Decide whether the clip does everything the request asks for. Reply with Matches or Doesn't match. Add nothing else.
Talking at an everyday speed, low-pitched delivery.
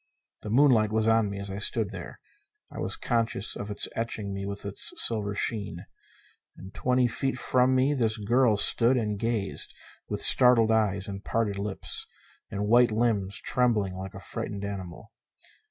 Matches